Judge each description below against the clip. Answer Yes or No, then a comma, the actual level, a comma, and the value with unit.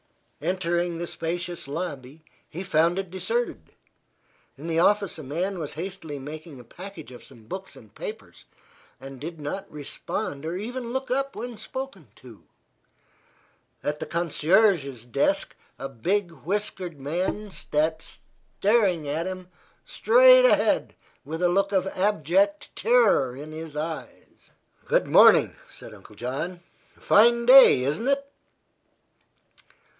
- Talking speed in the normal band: No, slow, 130 wpm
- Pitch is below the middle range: No, medium, 175 Hz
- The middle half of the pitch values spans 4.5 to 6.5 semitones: Yes, average, 5.3 semitones